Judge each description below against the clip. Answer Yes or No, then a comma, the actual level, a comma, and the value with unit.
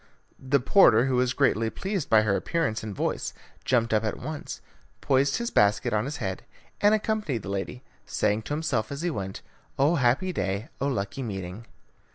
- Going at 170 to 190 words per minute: Yes, average, 185 wpm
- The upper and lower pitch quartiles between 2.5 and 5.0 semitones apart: No, wide, 5.5 semitones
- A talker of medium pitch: No, low, 125 Hz